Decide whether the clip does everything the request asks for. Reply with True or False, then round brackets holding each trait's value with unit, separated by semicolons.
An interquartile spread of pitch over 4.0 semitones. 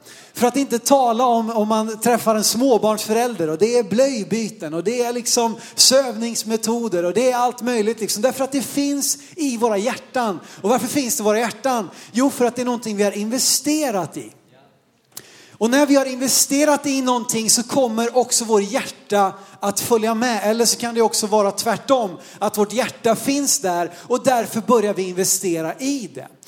False (3.3 semitones)